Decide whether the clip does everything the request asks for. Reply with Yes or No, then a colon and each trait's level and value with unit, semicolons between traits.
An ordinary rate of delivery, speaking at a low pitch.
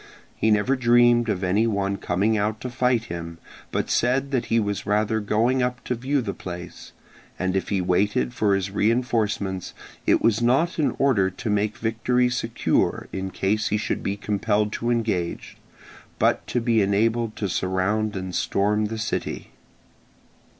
Yes: average, 165 wpm; low, 110 Hz